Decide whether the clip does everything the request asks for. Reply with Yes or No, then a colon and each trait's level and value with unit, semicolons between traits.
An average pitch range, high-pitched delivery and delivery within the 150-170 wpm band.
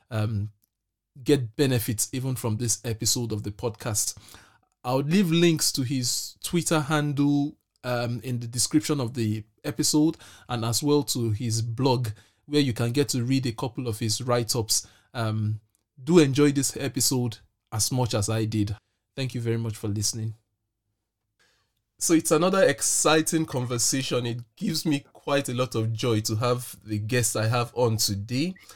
No: average, 4.0 semitones; low, 120 Hz; average, 165 wpm